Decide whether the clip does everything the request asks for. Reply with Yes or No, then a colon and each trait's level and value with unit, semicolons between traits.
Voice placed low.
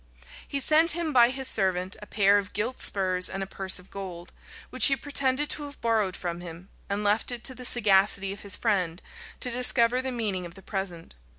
No: high, 205 Hz